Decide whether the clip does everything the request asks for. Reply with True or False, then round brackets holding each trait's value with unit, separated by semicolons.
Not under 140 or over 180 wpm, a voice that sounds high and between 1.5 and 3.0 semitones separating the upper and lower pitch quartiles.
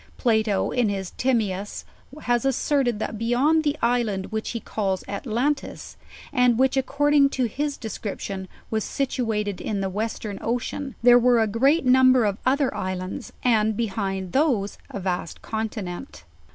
False (145 wpm; 230 Hz; 4.2 semitones)